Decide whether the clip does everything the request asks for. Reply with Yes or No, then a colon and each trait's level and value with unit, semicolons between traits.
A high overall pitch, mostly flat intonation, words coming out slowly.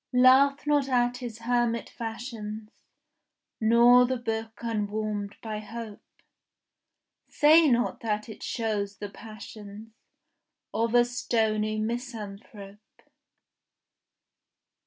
Yes: high, 225 Hz; narrow, 2.3 semitones; slow, 95 wpm